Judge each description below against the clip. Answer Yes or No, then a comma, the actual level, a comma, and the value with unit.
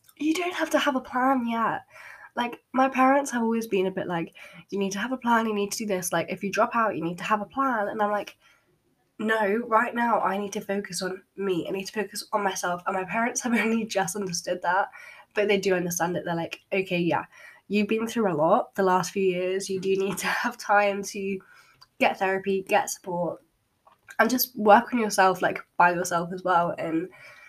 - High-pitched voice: Yes, high, 200 Hz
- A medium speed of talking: No, fast, 230 wpm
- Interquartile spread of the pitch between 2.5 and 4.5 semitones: Yes, average, 3.6 semitones